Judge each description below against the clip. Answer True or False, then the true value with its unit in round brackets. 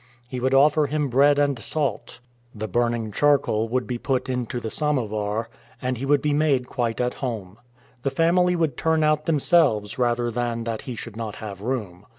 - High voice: False (125 Hz)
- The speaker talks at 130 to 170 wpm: False (185 wpm)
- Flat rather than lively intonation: False (4.3 semitones)